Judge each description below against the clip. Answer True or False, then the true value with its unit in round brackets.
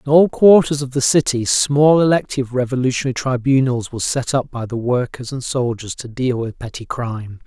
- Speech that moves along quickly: False (185 wpm)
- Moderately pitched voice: False (130 Hz)